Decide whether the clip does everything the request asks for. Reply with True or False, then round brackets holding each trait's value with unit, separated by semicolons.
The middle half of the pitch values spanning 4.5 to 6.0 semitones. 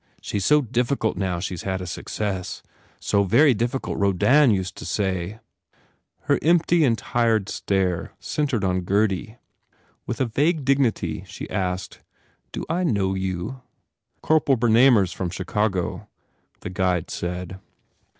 True (5.4 semitones)